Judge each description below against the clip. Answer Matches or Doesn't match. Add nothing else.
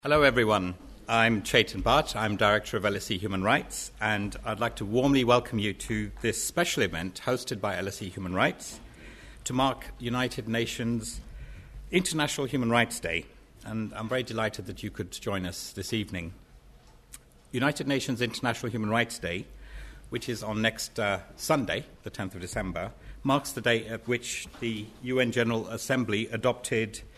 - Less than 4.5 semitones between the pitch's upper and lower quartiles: Matches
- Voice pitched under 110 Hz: Doesn't match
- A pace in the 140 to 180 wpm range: Matches